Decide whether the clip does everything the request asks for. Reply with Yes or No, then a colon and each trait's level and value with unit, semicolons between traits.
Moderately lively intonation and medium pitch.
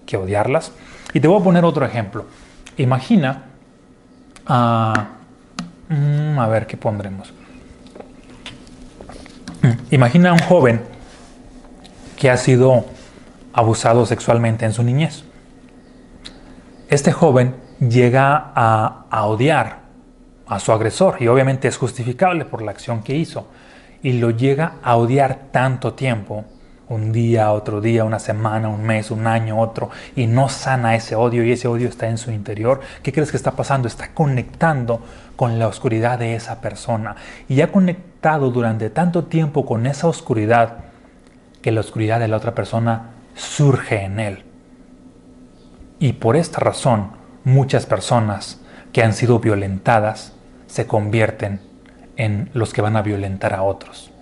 No: average, 3.4 semitones; low, 120 Hz